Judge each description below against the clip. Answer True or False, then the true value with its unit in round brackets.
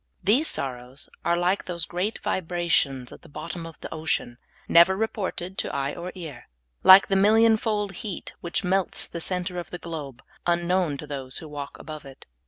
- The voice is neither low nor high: True (175 Hz)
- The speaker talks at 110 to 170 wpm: False (190 wpm)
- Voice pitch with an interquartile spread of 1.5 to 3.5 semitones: False (4.3 semitones)